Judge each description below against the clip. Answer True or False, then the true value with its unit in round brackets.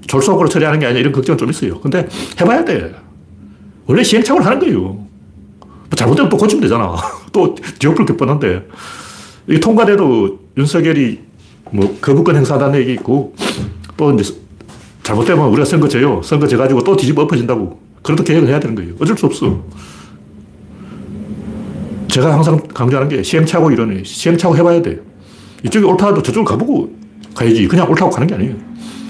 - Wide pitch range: True (7.2 semitones)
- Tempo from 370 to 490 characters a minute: True (375 characters per minute)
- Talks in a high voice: False (140 Hz)